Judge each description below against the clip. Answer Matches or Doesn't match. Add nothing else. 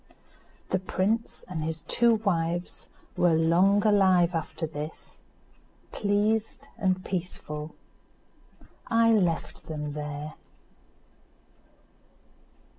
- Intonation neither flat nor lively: Matches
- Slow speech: Matches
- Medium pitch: Matches